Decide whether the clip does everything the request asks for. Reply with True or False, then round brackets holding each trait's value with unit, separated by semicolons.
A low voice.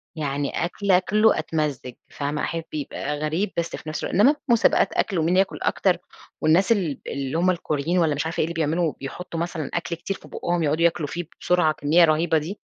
False (165 Hz)